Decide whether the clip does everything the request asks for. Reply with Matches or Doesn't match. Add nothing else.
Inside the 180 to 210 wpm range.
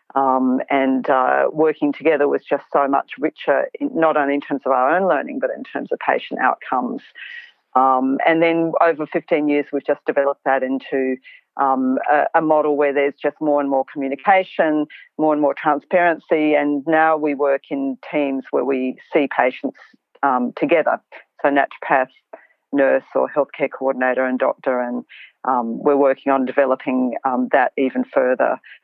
Doesn't match